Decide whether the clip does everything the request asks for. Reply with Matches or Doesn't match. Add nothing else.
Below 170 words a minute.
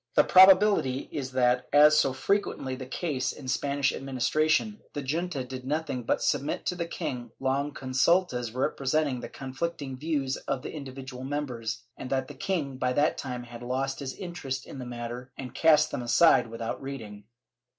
Doesn't match